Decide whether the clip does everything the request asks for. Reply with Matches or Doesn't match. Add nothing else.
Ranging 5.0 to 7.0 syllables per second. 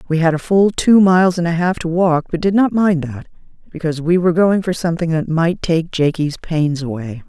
Matches